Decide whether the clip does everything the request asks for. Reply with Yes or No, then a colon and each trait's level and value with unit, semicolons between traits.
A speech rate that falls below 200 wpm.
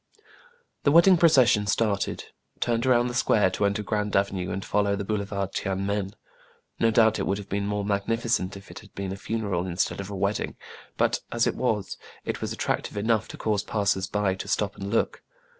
No: fast, 205 wpm